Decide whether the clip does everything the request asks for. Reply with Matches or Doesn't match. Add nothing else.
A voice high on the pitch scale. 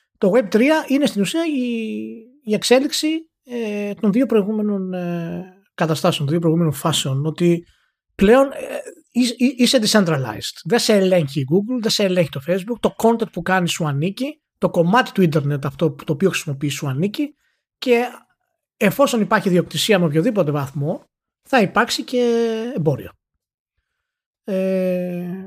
Matches